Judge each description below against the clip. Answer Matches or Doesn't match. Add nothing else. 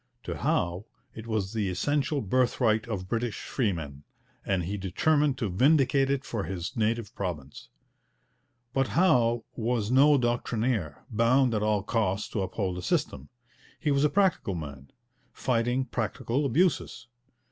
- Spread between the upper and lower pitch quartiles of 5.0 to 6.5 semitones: Matches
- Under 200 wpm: Matches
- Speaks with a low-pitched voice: Matches